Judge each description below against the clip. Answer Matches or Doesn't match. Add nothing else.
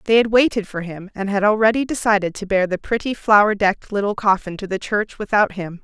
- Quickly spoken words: Matches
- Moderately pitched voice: Doesn't match